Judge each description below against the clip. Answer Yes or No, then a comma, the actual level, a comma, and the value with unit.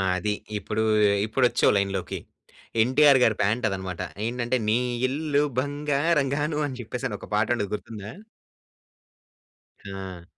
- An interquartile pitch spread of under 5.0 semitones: No, wide, 5.6 semitones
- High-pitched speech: No, low, 115 Hz